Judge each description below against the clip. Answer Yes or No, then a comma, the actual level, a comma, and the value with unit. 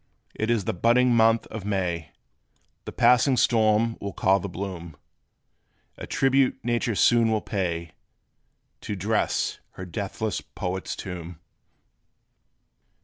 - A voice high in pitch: No, low, 105 Hz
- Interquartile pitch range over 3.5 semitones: Yes, average, 4.2 semitones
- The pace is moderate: No, slow, 120 wpm